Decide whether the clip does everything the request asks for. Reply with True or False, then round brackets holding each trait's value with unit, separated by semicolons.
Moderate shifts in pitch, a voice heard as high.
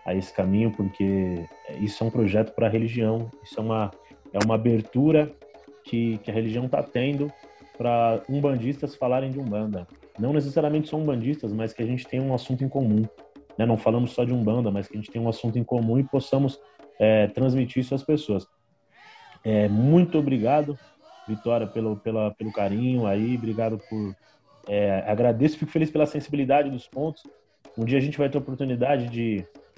False (4.1 semitones; 120 Hz)